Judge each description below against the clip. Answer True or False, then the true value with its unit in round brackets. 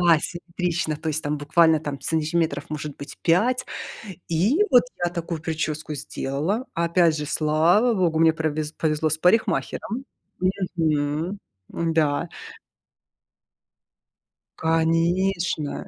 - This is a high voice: False (160 Hz)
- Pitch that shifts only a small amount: True (2.3 semitones)